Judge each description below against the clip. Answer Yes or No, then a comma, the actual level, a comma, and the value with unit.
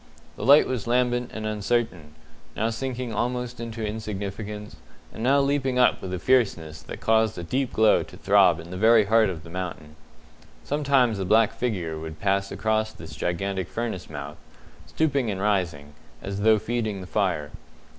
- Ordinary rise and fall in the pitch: Yes, average, 4.6 semitones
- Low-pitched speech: Yes, low, 110 Hz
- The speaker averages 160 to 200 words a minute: Yes, average, 170 wpm